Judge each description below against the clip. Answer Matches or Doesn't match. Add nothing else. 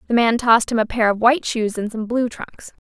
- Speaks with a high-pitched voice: Matches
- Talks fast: Matches